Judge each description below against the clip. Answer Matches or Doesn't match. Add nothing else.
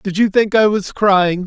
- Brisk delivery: Matches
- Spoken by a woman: Doesn't match